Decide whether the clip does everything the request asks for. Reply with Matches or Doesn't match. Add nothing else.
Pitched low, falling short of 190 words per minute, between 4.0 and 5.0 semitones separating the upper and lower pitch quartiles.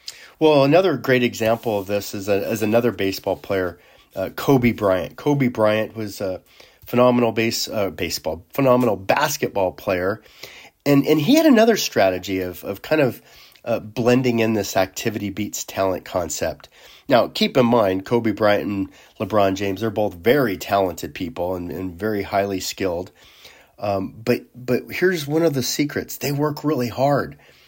Matches